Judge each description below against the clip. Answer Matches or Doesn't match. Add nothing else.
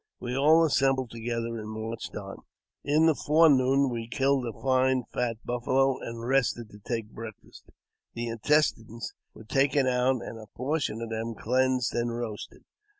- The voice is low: Matches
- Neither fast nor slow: Matches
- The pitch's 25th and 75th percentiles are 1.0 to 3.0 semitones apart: Matches